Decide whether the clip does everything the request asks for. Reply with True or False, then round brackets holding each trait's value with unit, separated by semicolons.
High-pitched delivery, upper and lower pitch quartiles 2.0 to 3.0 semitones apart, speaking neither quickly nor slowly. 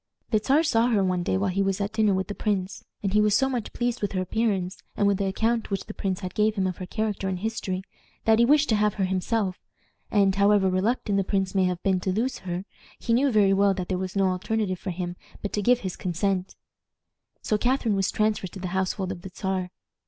False (195 Hz; 2.5 semitones; 240 wpm)